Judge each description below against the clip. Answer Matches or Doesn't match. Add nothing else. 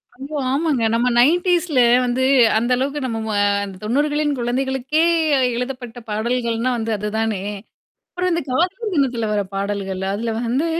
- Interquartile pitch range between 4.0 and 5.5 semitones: Matches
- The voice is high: Matches